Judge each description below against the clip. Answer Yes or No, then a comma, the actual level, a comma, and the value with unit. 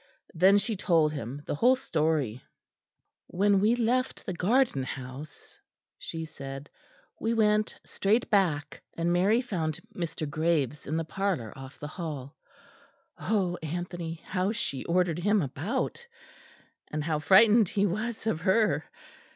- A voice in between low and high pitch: Yes, medium, 175 Hz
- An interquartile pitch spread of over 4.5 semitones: Yes, wide, 5.5 semitones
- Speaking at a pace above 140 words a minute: No, slow, 135 wpm